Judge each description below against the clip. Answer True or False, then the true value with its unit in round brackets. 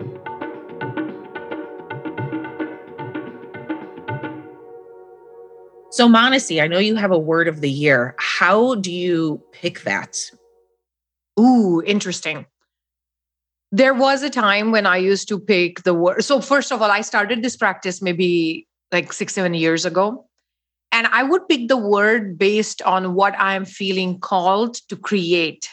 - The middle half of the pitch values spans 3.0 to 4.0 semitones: False (5.1 semitones)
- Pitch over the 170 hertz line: True (185 Hz)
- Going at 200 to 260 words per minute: False (135 wpm)